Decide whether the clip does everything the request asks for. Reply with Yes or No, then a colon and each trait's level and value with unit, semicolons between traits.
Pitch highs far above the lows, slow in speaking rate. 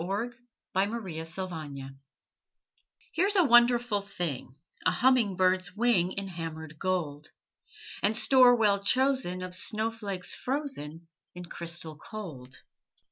Yes: wide, 6.0 semitones; slow, 110 wpm